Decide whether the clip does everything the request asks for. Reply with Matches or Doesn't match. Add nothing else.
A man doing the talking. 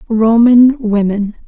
Doesn't match